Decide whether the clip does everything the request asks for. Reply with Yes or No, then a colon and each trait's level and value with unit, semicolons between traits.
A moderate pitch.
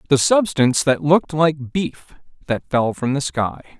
Yes: medium, 145 Hz